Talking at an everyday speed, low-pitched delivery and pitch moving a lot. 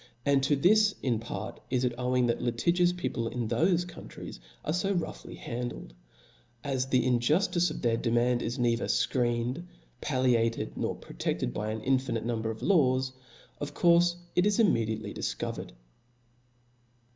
Yes: average, 150 wpm; low, 125 Hz; wide, 6.3 semitones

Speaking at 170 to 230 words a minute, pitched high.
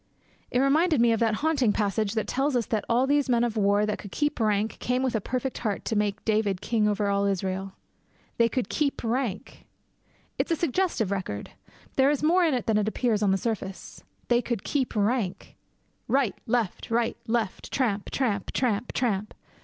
Yes: average, 190 wpm; high, 225 Hz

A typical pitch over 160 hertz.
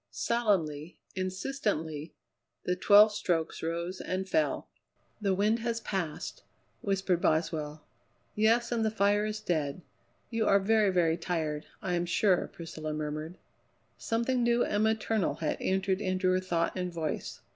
Yes: medium, 185 Hz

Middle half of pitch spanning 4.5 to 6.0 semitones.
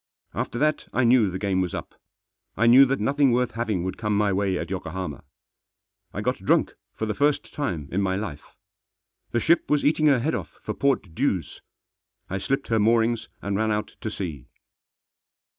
Yes: wide, 5.5 semitones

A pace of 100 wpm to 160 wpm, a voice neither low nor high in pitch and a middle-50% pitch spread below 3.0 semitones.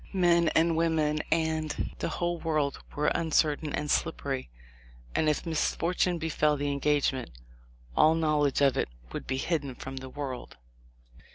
Yes: average, 145 wpm; medium, 155 Hz; narrow, 2.4 semitones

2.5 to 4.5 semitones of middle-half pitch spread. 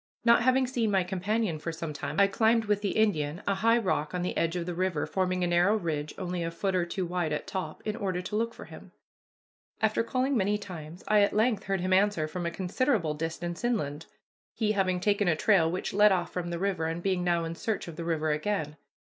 Yes: average, 3.7 semitones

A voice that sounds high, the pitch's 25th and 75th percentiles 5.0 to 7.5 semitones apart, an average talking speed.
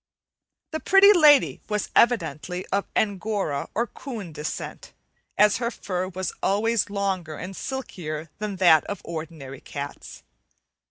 No: high, 195 Hz; wide, 5.5 semitones; slow, 125 wpm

